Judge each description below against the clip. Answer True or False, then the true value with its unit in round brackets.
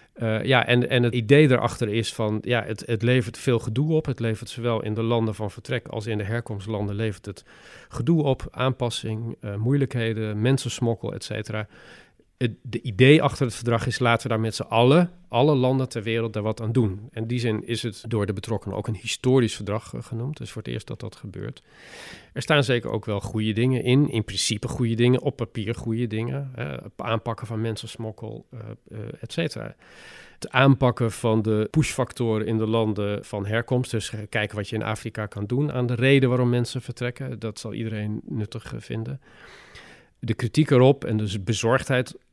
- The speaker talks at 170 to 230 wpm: True (195 wpm)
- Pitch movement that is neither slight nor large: False (2.3 semitones)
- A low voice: True (115 Hz)